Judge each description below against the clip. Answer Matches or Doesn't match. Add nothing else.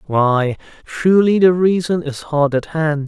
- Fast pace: Doesn't match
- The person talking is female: Doesn't match